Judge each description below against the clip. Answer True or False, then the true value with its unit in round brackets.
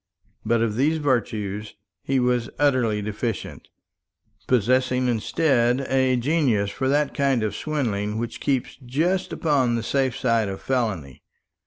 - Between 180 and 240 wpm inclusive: False (135 wpm)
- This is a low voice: True (125 Hz)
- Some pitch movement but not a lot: True (3.6 semitones)